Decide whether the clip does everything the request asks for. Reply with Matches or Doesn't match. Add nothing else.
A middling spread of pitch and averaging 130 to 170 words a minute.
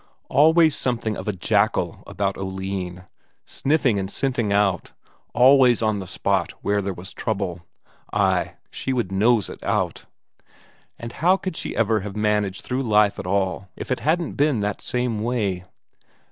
Matches